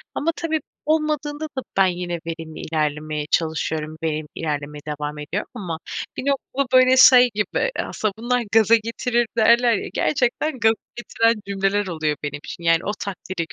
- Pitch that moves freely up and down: Yes, wide, 7.8 semitones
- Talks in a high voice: Yes, high, 200 Hz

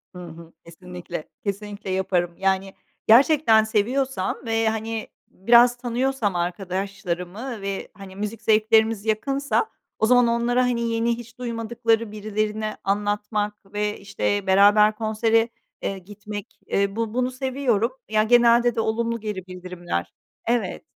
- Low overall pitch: No, high, 215 Hz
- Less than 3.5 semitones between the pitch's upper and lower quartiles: Yes, average, 2.9 semitones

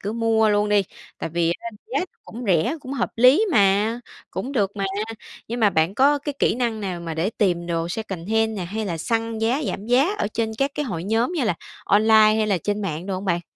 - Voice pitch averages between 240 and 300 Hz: No, high, 215 Hz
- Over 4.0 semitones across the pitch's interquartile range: No, average, 3.7 semitones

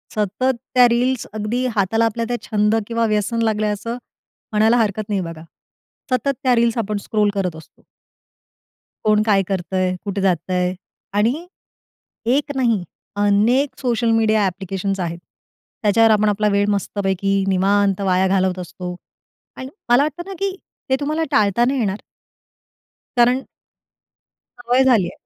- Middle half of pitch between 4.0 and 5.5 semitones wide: No, average, 3.5 semitones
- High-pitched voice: Yes, high, 210 Hz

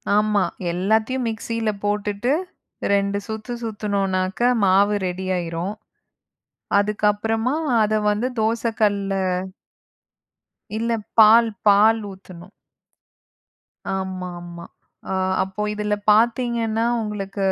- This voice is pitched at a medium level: No, high, 210 Hz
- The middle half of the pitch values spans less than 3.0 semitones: Yes, narrow, 2.6 semitones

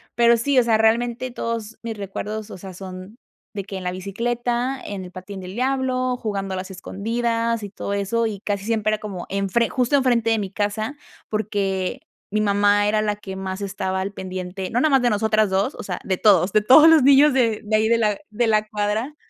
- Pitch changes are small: No, average, 3.1 semitones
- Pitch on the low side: No, high, 215 Hz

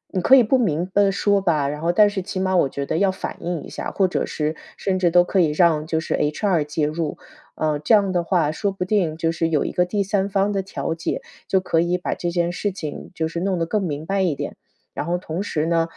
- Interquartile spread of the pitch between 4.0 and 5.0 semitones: No, average, 3.3 semitones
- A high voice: No, medium, 175 Hz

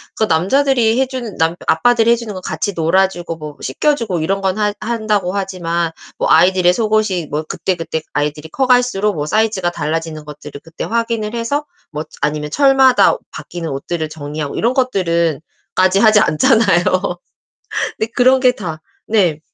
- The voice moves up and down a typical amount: No, wide, 6.0 semitones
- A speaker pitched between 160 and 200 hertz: Yes, high, 190 Hz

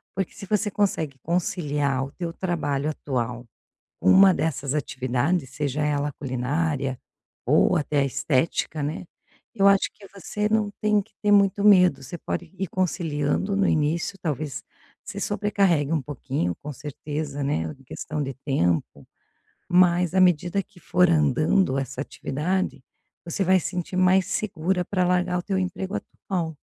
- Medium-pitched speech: Yes, medium, 165 Hz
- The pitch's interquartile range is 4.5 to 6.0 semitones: Yes, average, 4.8 semitones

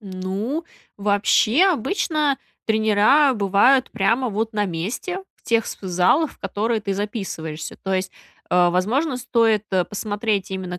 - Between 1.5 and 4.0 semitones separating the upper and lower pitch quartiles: No, average, 4.4 semitones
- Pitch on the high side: Yes, high, 210 Hz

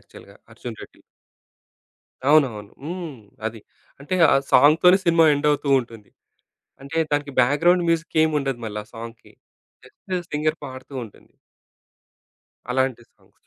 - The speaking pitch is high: No, medium, 145 Hz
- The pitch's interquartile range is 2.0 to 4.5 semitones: No, average, 5.0 semitones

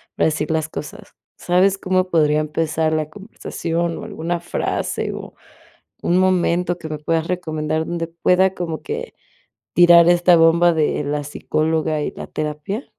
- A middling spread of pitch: No, narrow, 2.3 semitones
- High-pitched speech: No, medium, 165 Hz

